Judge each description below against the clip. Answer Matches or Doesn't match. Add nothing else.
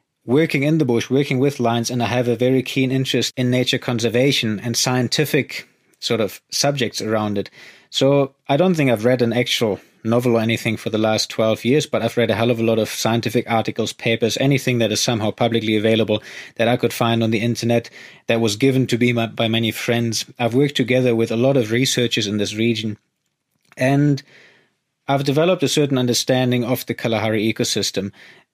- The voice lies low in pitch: Matches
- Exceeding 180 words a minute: Matches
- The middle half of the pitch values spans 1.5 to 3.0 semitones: Matches